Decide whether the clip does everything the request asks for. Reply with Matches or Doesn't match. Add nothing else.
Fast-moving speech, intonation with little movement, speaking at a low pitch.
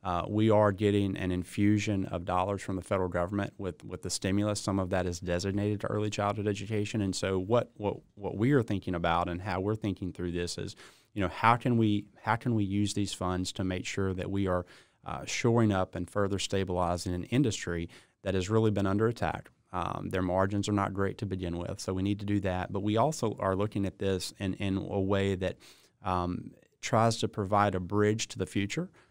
Matches